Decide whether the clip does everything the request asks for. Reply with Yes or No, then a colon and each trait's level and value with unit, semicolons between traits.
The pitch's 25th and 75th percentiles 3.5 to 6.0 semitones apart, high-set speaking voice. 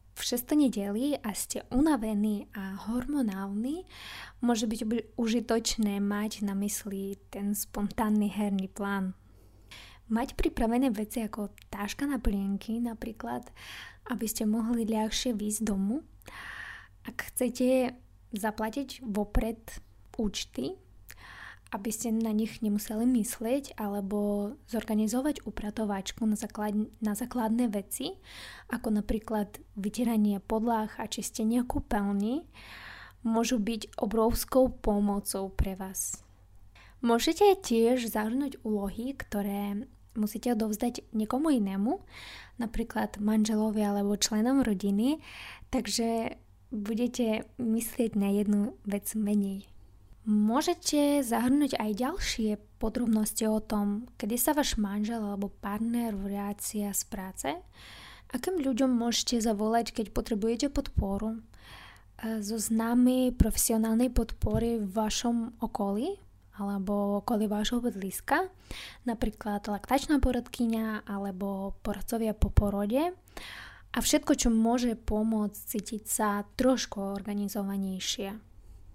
No: average, 2.8 semitones; high, 220 Hz